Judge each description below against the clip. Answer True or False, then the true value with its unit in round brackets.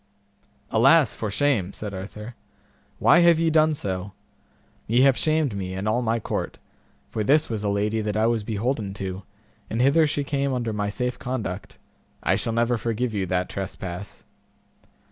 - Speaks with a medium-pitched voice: False (110 Hz)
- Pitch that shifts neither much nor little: True (4.5 semitones)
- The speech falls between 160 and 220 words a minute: True (170 wpm)